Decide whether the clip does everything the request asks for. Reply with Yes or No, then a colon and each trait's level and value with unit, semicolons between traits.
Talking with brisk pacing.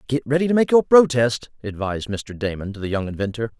Yes: fast, 215 wpm